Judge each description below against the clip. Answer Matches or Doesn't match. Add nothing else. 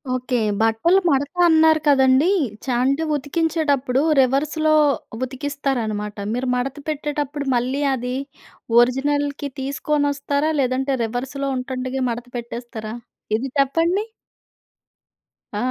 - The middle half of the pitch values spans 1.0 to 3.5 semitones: Matches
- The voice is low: Doesn't match